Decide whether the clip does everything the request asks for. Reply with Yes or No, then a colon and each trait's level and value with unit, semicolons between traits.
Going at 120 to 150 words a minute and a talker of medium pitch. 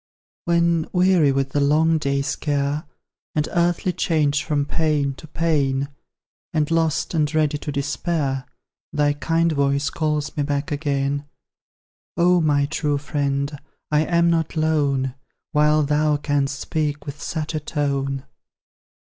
Yes: slow, 135 wpm; medium, 150 Hz